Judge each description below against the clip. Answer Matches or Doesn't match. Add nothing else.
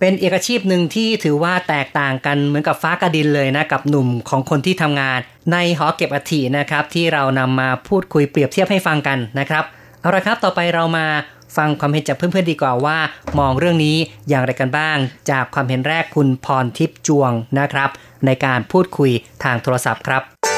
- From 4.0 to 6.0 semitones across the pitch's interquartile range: Doesn't match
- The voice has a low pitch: Doesn't match